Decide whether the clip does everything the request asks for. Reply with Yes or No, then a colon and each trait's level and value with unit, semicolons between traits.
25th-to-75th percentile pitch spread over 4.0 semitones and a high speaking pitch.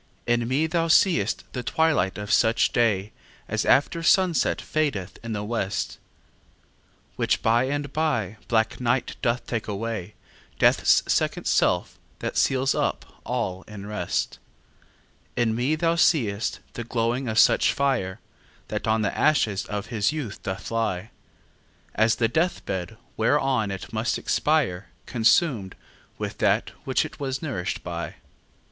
No: average, 5.0 semitones; low, 115 Hz